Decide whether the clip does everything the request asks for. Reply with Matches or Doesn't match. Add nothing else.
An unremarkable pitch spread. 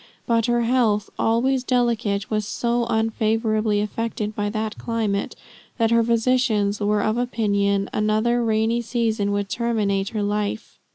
Doesn't match